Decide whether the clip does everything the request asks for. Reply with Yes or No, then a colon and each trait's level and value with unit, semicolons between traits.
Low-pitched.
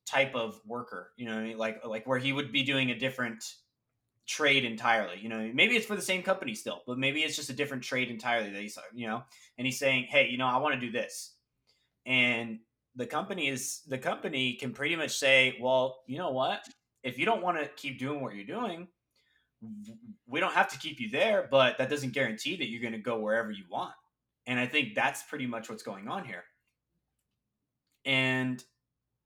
Yes: low, 130 Hz